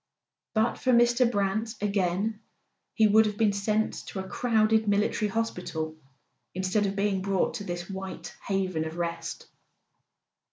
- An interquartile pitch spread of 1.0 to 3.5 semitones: Yes, narrow, 2.6 semitones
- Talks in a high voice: Yes, high, 200 Hz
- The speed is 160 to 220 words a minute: No, average, 145 wpm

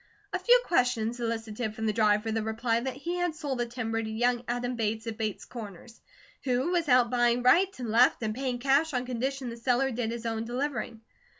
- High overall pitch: Yes, high, 240 Hz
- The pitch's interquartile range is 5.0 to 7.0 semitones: No, narrow, 2.4 semitones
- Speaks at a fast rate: Yes, fast, 210 wpm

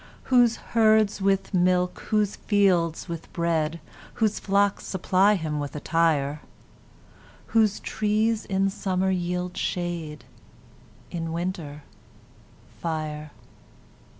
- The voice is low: No, medium, 180 Hz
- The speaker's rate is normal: No, slow, 95 wpm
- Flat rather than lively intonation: No, average, 3.7 semitones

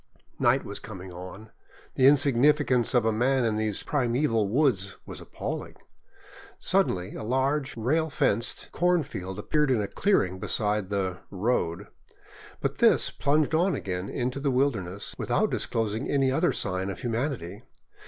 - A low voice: Yes, low, 120 Hz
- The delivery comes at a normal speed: Yes, average, 145 wpm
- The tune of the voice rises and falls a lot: Yes, wide, 6.1 semitones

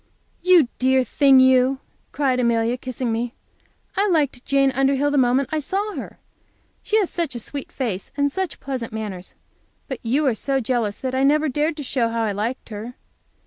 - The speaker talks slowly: No, average, 185 wpm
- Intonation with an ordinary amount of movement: Yes, average, 3.3 semitones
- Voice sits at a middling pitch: No, very high, 260 Hz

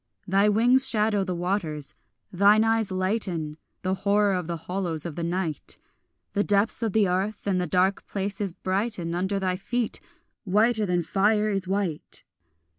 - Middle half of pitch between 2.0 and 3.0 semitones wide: Yes, narrow, 2.6 semitones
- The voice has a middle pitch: No, high, 195 Hz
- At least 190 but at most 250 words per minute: No, average, 160 wpm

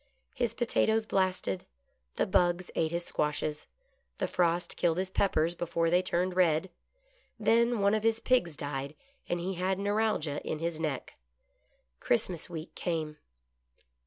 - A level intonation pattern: No, average, 3.9 semitones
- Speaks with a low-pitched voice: No, medium, 175 Hz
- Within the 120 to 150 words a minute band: Yes, average, 140 wpm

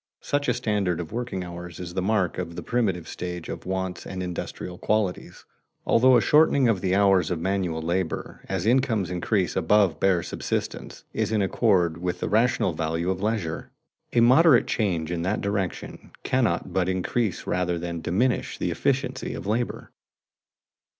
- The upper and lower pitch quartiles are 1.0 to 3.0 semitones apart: No, average, 3.8 semitones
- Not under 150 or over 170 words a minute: Yes, average, 165 wpm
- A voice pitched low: Yes, very low, 95 Hz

